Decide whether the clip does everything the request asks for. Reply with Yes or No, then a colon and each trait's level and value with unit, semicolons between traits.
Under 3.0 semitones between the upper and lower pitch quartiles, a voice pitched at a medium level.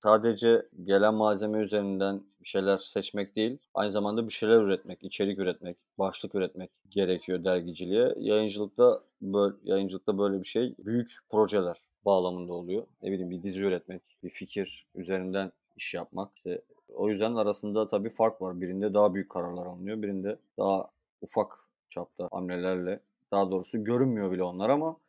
No: narrow, 2.6 semitones; low, 100 Hz